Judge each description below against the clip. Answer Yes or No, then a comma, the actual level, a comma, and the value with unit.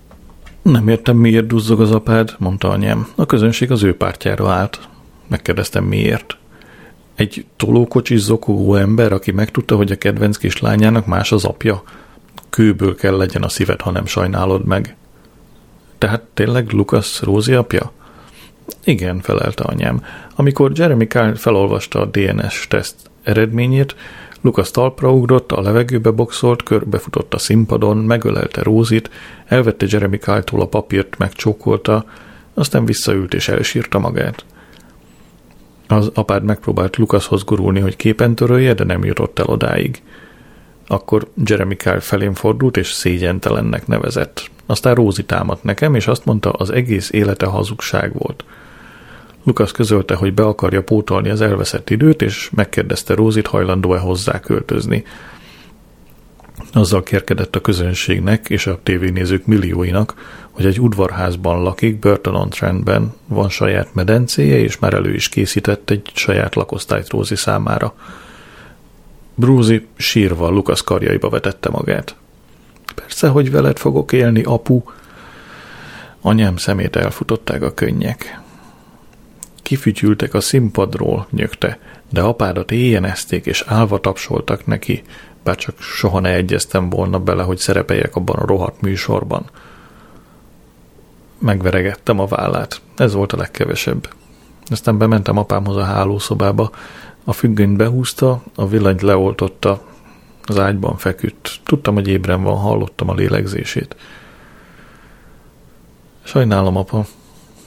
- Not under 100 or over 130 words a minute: Yes, average, 125 wpm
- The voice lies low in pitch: Yes, low, 105 Hz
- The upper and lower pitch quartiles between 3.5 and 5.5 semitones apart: No, average, 2.9 semitones